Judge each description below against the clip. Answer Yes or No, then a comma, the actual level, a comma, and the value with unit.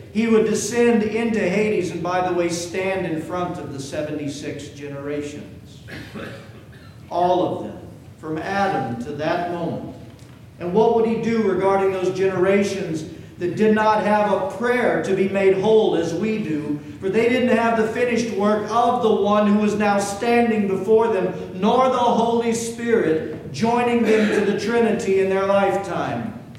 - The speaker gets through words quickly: No, average, 165 wpm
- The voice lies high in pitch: Yes, high, 195 Hz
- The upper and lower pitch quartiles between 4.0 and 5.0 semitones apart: Yes, average, 4.5 semitones